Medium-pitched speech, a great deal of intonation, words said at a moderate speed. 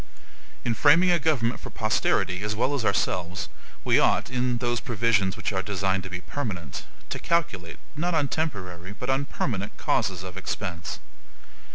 No: low, 110 Hz; wide, 6.1 semitones; average, 165 wpm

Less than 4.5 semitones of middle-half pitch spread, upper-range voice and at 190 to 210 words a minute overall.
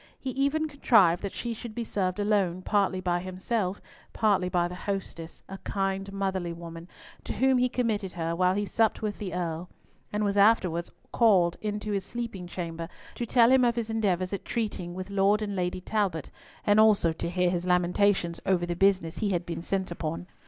Yes: average, 3.2 semitones; high, 195 Hz; average, 195 wpm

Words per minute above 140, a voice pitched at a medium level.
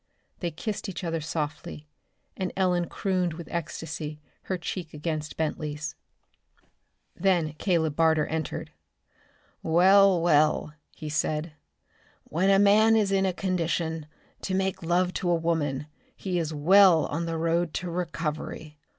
No: slow, 135 wpm; medium, 165 Hz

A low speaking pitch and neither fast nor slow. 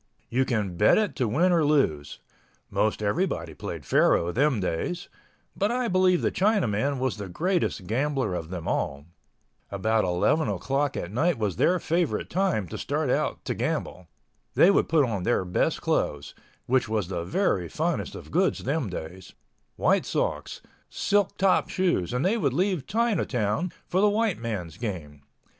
Yes: low, 125 Hz; average, 160 wpm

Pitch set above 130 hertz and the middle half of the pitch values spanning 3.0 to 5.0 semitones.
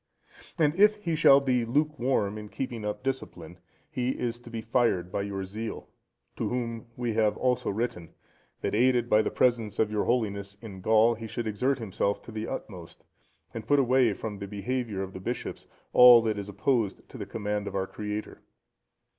No: low, 115 Hz; average, 3.3 semitones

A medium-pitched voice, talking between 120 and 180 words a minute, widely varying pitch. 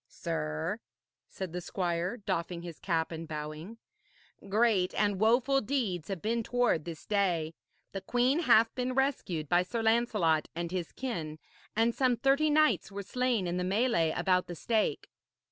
No: high, 195 Hz; average, 160 wpm; wide, 5.9 semitones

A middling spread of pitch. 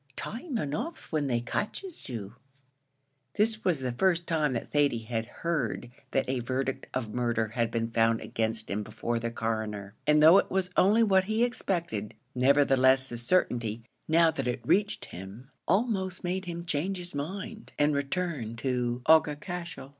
No: wide, 7.4 semitones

